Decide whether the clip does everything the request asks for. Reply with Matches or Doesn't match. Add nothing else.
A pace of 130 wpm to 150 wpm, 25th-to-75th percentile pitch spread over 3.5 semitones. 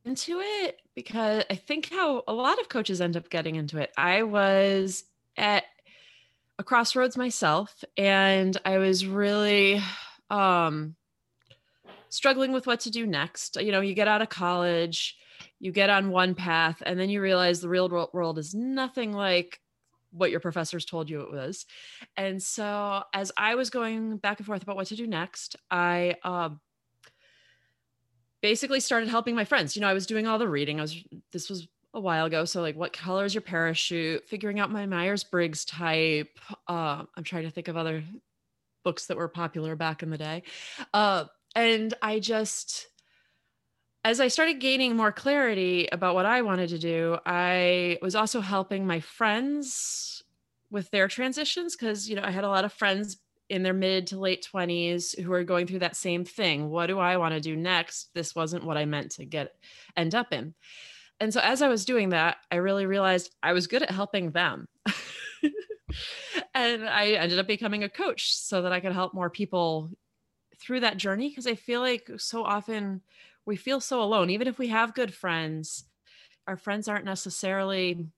Doesn't match